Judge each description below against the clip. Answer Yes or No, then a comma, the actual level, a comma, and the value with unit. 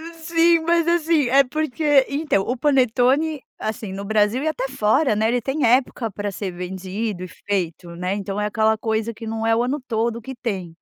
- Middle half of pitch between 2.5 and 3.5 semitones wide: No, average, 5.1 semitones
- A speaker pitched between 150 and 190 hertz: No, high, 230 Hz